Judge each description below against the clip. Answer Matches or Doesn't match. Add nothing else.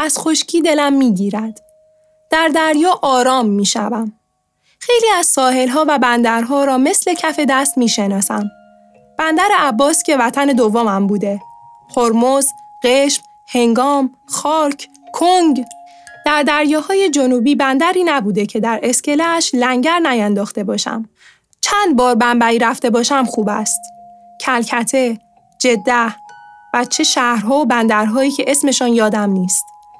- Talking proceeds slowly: Doesn't match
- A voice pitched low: Doesn't match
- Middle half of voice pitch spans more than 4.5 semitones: Matches